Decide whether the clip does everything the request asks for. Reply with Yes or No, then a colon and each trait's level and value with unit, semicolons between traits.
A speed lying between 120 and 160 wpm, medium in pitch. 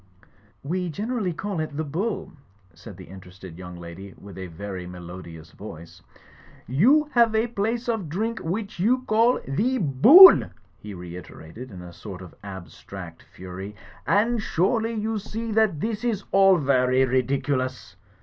Yes: average, 150 wpm; medium, 145 Hz